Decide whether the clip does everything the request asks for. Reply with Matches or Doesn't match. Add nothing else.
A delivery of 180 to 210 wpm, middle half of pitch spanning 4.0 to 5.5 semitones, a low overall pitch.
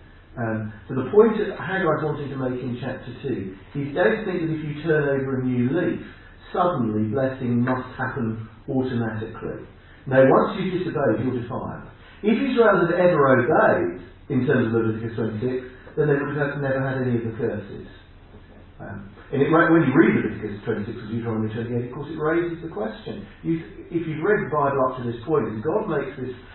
Matches